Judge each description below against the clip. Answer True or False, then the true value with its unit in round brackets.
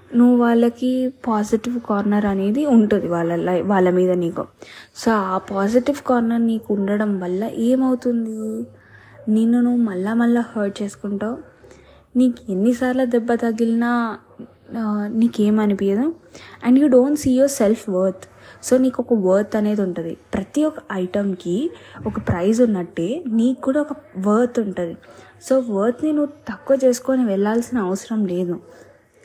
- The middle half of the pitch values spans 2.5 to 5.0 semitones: True (3.7 semitones)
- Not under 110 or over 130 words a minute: True (125 wpm)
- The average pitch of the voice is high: True (225 Hz)